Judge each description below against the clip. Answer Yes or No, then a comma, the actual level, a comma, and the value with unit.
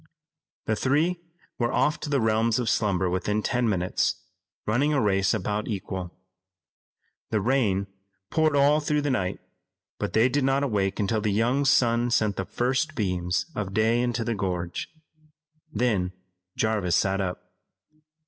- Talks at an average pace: Yes, average, 150 wpm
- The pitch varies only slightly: No, average, 5.0 semitones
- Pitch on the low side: Yes, low, 110 Hz